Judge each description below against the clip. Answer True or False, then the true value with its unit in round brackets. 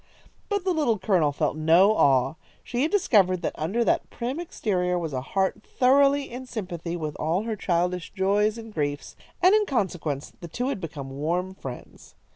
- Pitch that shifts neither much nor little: False (6.9 semitones)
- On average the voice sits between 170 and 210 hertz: True (190 Hz)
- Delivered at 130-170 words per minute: False (180 wpm)